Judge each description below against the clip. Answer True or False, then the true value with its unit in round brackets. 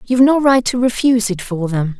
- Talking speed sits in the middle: False (240 wpm)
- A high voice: True (225 Hz)